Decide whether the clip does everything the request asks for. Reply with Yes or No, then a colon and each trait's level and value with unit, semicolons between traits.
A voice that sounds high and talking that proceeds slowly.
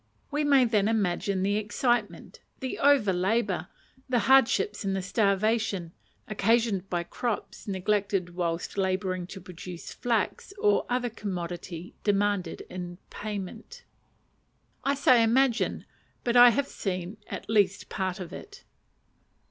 Yes: high, 205 Hz; slow, 125 wpm